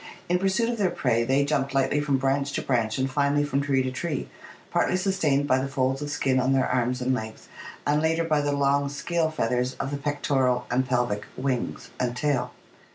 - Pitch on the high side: No, medium, 140 Hz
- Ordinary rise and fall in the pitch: No, narrow, 2.3 semitones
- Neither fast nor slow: No, fast, 210 wpm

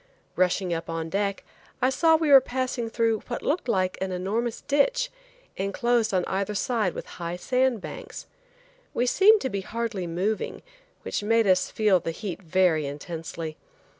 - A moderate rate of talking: Yes, average, 165 wpm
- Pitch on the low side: No, high, 205 Hz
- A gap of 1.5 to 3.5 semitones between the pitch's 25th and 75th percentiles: No, average, 5.1 semitones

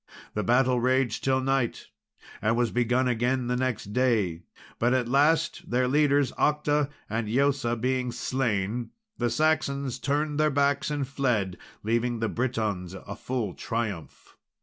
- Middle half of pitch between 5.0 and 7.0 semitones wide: No, average, 3.2 semitones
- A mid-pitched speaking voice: No, low, 125 Hz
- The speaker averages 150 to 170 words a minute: No, average, 140 wpm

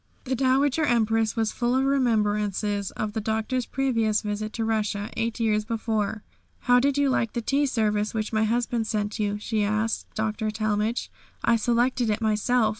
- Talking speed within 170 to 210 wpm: Yes, average, 175 wpm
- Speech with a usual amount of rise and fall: No, narrow, 2.3 semitones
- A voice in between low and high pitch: No, high, 220 Hz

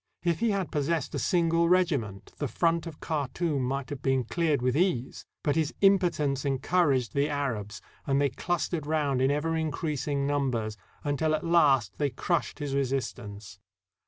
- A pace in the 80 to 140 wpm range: No, average, 160 wpm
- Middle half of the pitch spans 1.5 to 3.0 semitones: No, average, 3.8 semitones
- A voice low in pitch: No, medium, 145 Hz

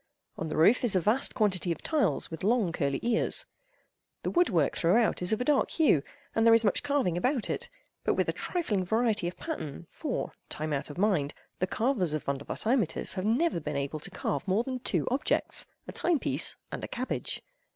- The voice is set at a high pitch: Yes, high, 210 Hz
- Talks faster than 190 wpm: Yes, average, 200 wpm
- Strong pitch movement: Yes, wide, 7.3 semitones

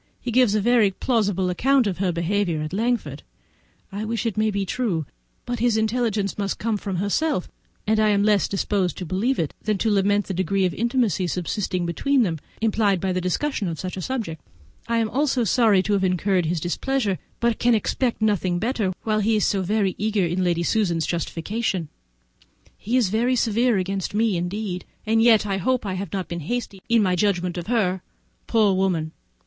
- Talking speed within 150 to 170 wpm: No, average, 195 wpm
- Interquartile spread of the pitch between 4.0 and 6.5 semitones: No, average, 3.6 semitones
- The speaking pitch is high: Yes, high, 205 Hz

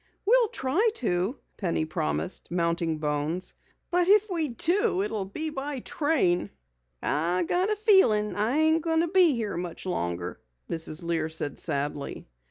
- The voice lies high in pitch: Yes, high, 205 Hz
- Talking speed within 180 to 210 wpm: No, average, 155 wpm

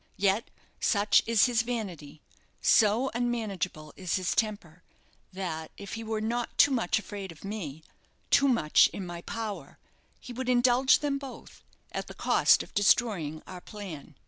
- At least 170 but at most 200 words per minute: No, average, 155 wpm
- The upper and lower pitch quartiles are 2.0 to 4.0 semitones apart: No, average, 5.1 semitones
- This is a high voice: Yes, high, 210 Hz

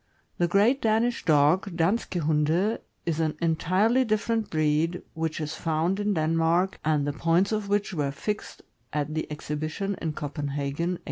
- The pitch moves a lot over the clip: No, average, 4.6 semitones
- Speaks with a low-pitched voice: No, medium, 165 Hz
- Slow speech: No, average, 155 wpm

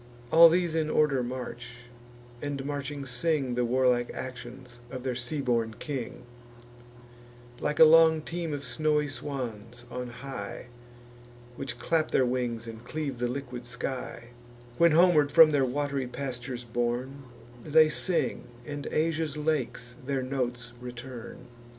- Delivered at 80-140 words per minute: Yes, slow, 135 wpm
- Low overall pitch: Yes, low, 130 Hz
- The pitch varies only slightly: No, average, 3.5 semitones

